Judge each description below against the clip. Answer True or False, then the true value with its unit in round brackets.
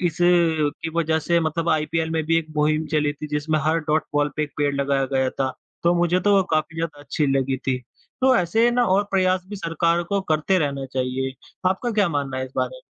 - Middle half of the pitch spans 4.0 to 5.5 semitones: False (3.2 semitones)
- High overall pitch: False (160 Hz)